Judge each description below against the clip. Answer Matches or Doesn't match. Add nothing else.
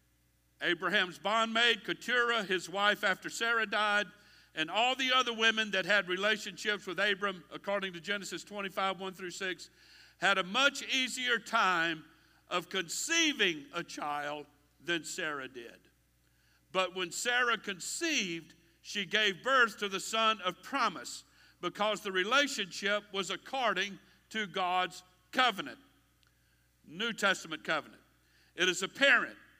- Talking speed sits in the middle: Doesn't match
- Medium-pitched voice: Doesn't match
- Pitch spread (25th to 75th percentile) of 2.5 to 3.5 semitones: Doesn't match